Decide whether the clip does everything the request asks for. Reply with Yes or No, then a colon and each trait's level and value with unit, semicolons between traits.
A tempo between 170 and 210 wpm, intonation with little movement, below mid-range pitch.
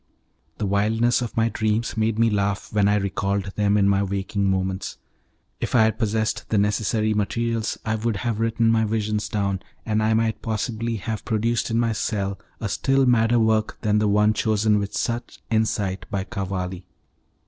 Yes: average, 180 wpm; narrow, 2.0 semitones; low, 110 Hz